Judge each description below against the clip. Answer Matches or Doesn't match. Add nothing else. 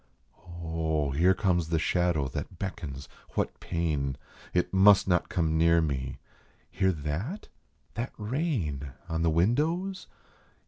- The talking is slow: Matches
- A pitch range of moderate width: Matches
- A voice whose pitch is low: Matches